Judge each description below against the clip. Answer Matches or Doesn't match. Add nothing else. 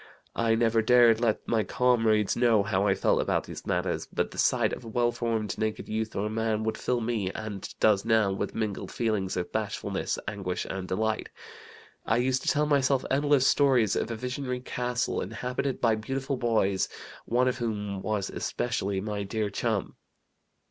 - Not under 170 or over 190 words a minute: Matches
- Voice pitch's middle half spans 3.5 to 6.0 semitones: Doesn't match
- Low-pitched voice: Matches